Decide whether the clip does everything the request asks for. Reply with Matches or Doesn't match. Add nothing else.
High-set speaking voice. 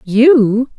Matches